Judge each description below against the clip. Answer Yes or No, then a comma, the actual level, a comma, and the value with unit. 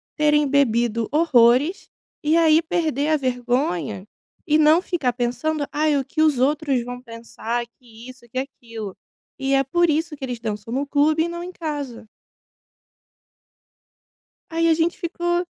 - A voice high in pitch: Yes, very high, 280 Hz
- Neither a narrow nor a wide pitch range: Yes, average, 4.6 semitones